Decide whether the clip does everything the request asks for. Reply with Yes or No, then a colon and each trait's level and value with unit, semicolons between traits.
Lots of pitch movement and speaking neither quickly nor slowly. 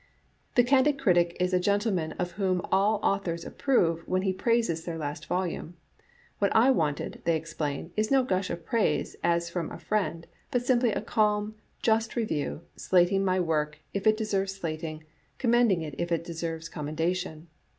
No: average, 4.4 semitones; average, 180 wpm